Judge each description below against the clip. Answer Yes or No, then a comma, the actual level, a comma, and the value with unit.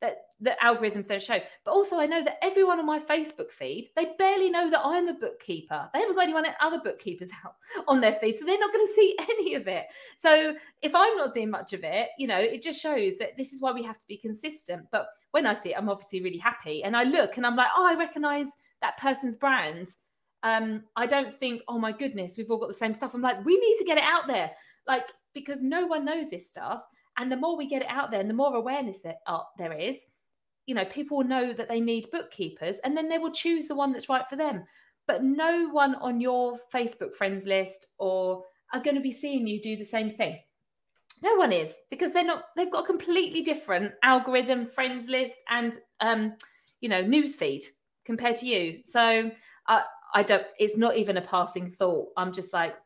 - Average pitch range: No, wide, 6.5 semitones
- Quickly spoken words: Yes, fast, 230 wpm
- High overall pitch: Yes, very high, 260 Hz